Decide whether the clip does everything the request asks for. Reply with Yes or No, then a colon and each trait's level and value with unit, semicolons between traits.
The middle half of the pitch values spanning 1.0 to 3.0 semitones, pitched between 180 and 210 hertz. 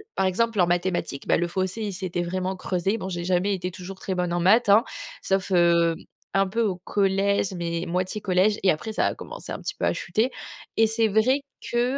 Yes: average, 2.7 semitones; high, 190 Hz